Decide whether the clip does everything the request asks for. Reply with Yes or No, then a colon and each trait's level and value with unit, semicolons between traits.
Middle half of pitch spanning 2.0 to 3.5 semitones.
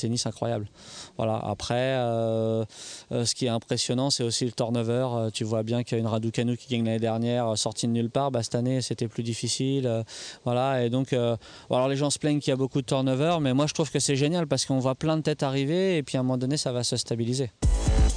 Yes: average, 2.8 semitones